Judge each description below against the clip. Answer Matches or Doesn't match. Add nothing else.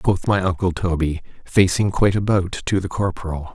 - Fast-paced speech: Doesn't match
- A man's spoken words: Matches